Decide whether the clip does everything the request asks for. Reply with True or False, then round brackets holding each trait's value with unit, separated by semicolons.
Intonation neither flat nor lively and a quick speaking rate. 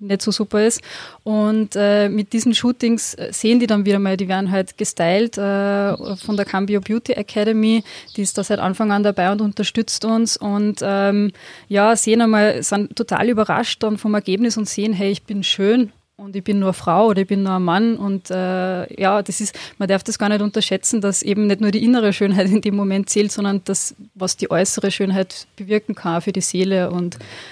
False (1.8 semitones; 210 wpm)